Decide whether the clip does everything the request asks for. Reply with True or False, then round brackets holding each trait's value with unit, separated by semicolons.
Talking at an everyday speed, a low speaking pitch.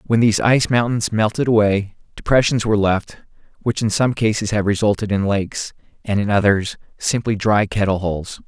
True (170 wpm; 105 Hz)